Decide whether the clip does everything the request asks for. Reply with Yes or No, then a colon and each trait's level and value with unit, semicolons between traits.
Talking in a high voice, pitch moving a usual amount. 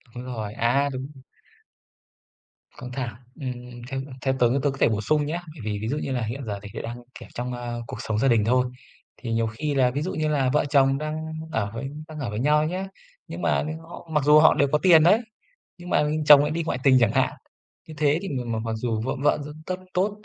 No: low, 135 Hz; average, 4.2 semitones